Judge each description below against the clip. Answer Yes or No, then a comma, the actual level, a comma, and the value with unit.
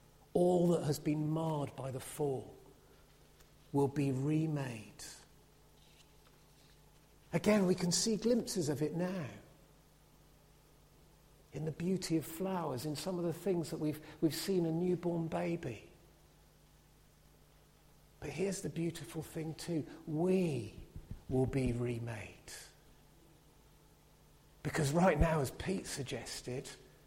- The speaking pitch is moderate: Yes, medium, 155 Hz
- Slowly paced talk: Yes, slow, 115 wpm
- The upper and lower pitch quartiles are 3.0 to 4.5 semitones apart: Yes, average, 3.4 semitones